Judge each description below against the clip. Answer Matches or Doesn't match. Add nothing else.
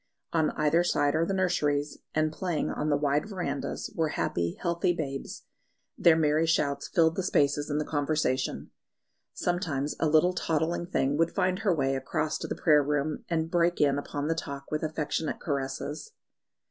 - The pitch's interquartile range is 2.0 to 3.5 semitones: Matches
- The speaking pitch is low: Doesn't match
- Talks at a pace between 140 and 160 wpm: Doesn't match